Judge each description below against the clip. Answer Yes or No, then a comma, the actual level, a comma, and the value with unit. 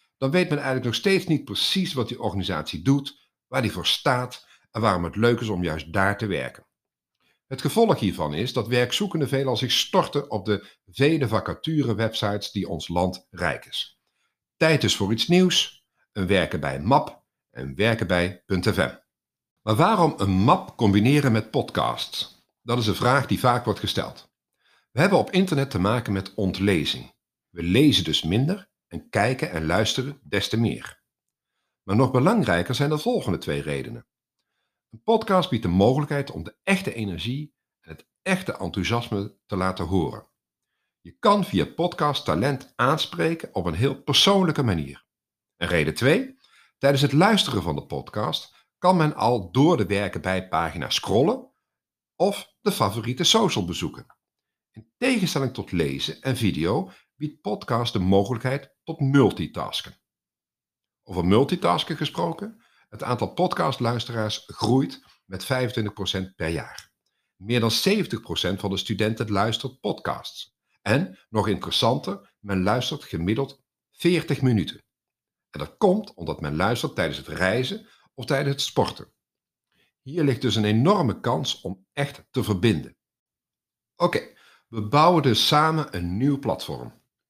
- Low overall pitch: Yes, low, 120 Hz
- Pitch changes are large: Yes, wide, 6.6 semitones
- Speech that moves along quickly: No, average, 155 wpm